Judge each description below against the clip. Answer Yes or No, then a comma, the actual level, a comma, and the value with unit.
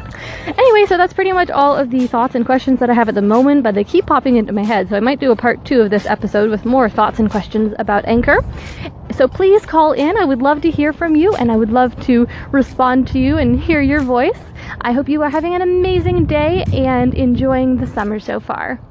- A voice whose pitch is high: Yes, very high, 260 Hz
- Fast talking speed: Yes, fast, 250 wpm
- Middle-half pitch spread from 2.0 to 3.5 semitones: No, average, 4.6 semitones